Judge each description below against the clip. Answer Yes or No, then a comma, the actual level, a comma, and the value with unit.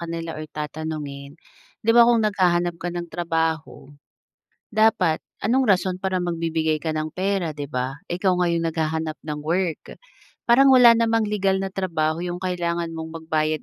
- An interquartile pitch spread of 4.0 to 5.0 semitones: No, average, 3.2 semitones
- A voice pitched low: No, medium, 170 Hz